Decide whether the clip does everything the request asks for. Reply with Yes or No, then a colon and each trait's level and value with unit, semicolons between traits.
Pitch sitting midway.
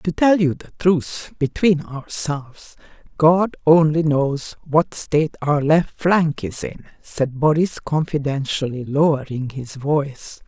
Yes: medium, 150 Hz